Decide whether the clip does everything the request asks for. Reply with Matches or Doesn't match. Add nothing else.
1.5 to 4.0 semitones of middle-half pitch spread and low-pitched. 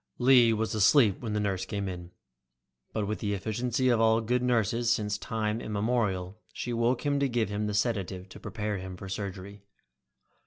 Matches